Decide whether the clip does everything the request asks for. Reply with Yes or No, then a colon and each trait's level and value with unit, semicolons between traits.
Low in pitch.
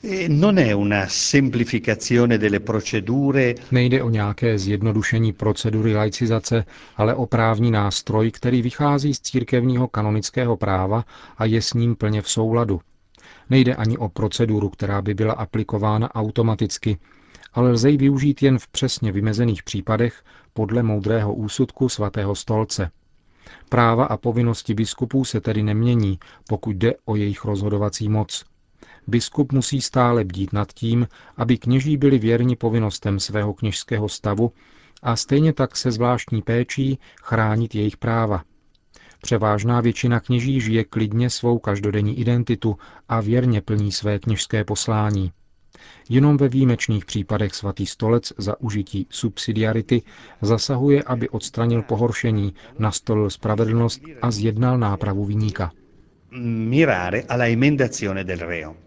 Yes: low, 115 Hz